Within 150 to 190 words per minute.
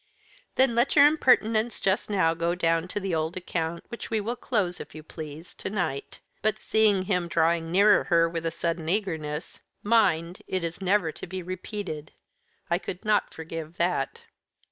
Yes: average, 175 wpm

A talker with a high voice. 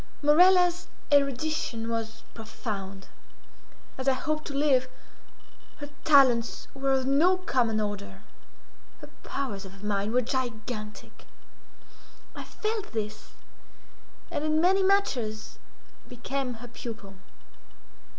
Yes: very high, 250 Hz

